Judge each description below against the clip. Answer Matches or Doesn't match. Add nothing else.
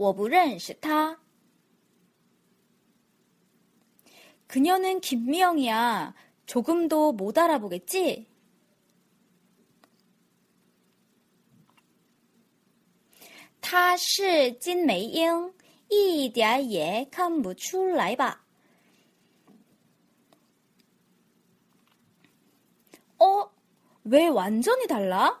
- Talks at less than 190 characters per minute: Matches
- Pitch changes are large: Matches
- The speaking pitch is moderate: Doesn't match